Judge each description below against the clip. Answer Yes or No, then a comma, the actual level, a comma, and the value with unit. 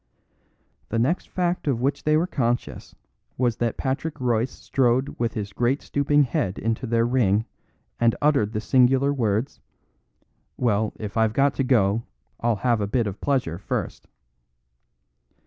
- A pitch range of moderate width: Yes, average, 3.6 semitones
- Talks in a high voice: No, low, 120 Hz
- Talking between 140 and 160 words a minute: Yes, average, 150 wpm